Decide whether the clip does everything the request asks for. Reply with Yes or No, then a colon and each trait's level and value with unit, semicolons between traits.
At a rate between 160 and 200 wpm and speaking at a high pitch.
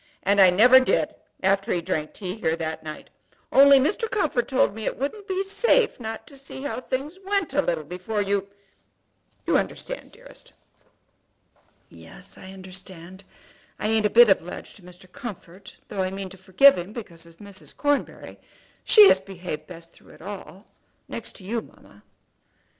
Yes: average, 170 wpm; high, 200 Hz